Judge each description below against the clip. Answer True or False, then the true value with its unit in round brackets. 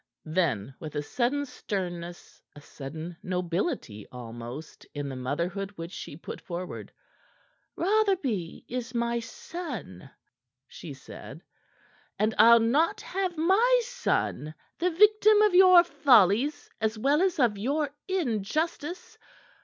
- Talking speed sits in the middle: False (120 wpm)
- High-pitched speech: True (225 Hz)